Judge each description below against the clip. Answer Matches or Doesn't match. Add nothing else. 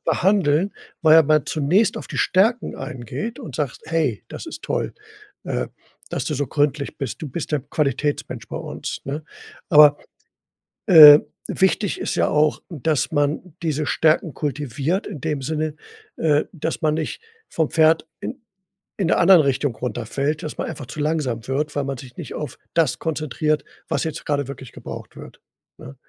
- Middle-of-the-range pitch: Matches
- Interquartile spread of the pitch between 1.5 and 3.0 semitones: Matches